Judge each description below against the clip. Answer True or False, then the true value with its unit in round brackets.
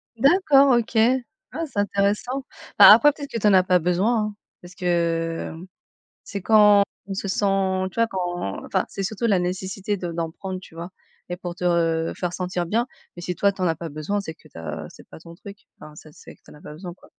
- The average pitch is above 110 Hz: True (185 Hz)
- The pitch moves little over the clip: False (3.1 semitones)